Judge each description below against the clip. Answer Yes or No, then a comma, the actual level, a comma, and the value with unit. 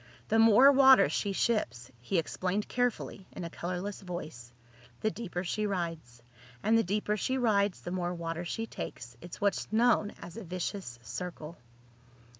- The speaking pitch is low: No, medium, 185 Hz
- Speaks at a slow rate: No, average, 160 wpm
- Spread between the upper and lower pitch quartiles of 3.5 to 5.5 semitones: Yes, average, 4.3 semitones